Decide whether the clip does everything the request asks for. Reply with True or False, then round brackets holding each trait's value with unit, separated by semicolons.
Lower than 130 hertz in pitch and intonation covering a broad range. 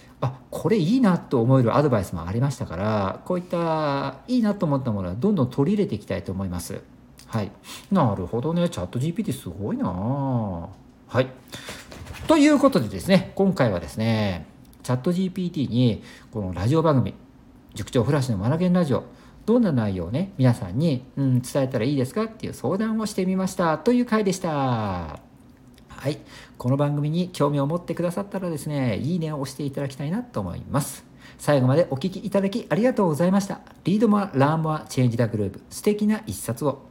False (140 Hz; 7.1 semitones)